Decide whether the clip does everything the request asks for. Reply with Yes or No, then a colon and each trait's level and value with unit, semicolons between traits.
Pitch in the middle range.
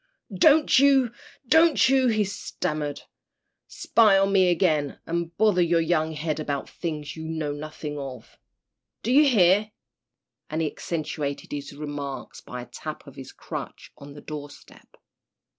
Yes: medium, 160 Hz